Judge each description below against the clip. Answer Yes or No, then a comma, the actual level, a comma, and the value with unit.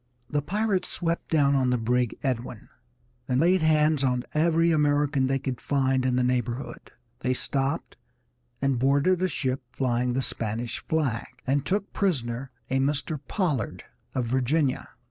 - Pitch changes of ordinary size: Yes, average, 3.6 semitones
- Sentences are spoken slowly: No, average, 150 wpm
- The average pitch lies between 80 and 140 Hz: Yes, low, 135 Hz